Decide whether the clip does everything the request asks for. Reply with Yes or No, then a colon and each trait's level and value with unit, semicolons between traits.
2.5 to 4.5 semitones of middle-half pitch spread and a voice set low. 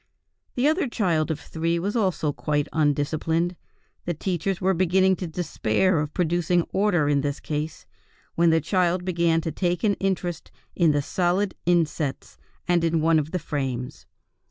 No: average, 3.0 semitones; medium, 170 Hz